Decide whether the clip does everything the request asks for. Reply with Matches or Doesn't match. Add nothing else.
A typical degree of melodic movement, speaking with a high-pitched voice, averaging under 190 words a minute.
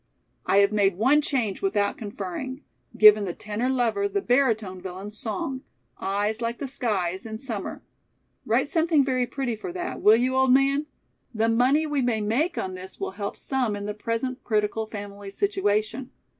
Matches